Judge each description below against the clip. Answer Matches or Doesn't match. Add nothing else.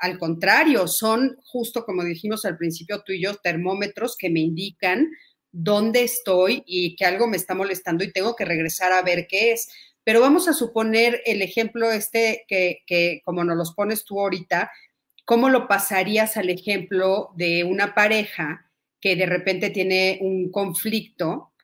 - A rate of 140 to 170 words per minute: Matches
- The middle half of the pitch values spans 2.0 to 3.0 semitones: Doesn't match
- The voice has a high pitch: Matches